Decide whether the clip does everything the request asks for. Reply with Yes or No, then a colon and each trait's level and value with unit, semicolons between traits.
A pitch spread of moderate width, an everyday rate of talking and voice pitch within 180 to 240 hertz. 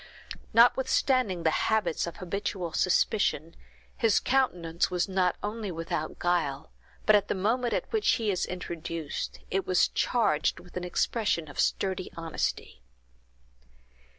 No: average, 4.5 semitones; slow, 130 wpm; medium, 185 Hz